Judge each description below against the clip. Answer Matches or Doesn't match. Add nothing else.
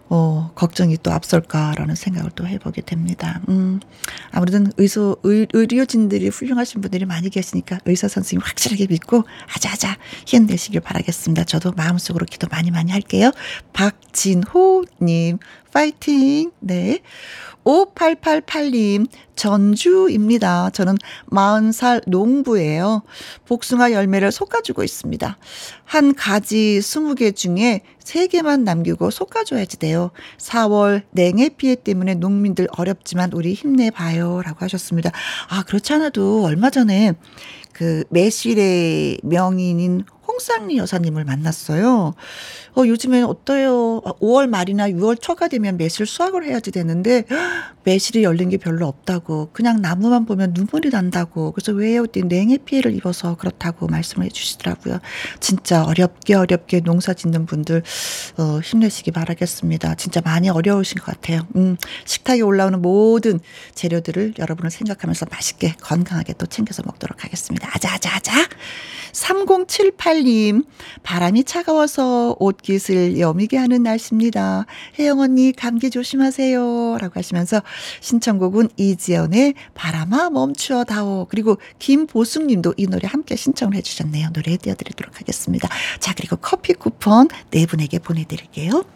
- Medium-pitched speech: Doesn't match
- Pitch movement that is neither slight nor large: Doesn't match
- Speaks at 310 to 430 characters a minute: Matches